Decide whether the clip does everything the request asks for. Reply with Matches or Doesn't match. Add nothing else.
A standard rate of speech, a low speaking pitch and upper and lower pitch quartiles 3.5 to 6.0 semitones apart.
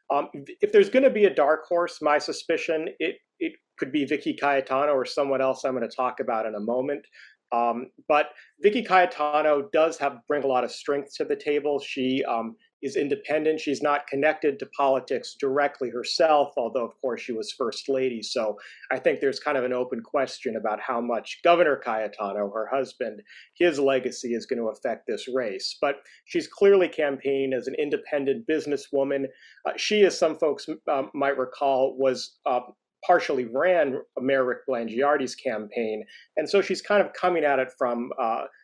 Doesn't match